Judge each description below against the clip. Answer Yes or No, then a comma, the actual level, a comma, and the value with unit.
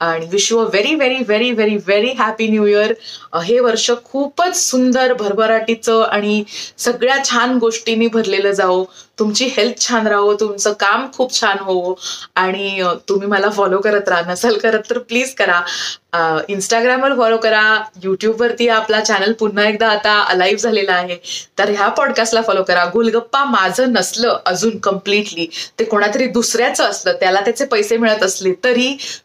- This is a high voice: Yes, high, 215 Hz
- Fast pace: Yes, fast, 150 wpm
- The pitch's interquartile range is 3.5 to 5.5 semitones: No, average, 3.0 semitones